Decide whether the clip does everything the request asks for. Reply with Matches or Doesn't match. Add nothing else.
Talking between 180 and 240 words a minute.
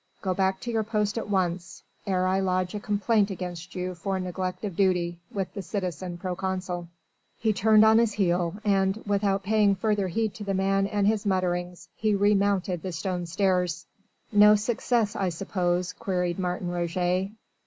Doesn't match